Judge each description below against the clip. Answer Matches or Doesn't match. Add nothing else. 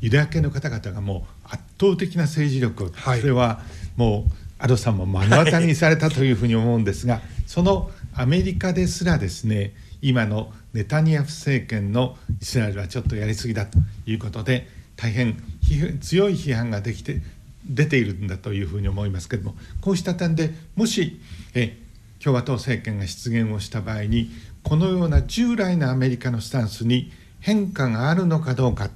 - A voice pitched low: Matches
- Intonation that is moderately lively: Doesn't match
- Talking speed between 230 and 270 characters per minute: Doesn't match